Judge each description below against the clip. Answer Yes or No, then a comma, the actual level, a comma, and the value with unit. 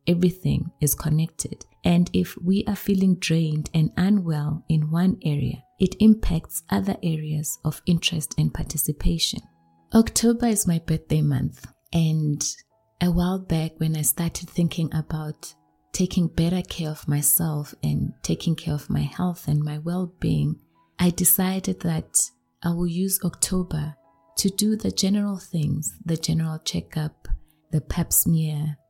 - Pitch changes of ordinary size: Yes, average, 3.0 semitones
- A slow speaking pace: No, average, 145 wpm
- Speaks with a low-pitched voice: No, medium, 160 Hz